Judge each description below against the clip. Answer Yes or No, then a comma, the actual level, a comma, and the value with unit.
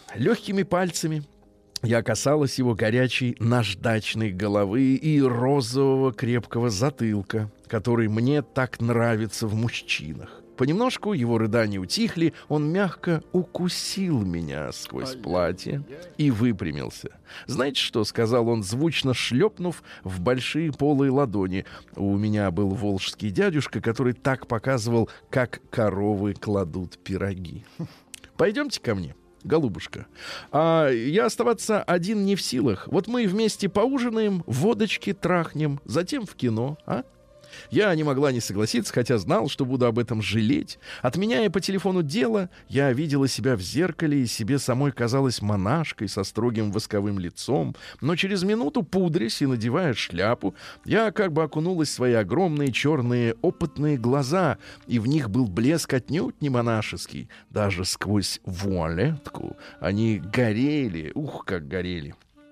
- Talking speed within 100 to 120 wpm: No, average, 130 wpm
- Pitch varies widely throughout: Yes, wide, 7.1 semitones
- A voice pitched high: No, low, 130 Hz